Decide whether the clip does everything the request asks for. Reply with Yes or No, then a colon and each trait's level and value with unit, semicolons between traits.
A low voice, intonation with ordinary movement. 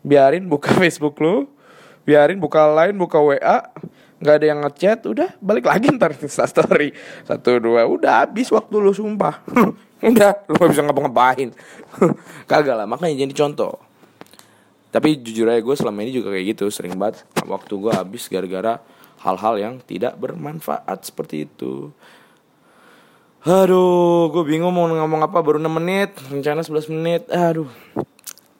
No: medium, 155 Hz; average, 4.4 semitones